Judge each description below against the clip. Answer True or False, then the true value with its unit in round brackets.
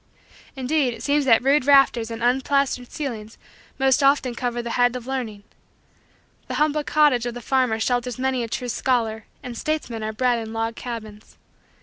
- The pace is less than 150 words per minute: False (175 wpm)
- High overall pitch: True (245 Hz)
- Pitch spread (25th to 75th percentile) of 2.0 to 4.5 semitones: True (2.7 semitones)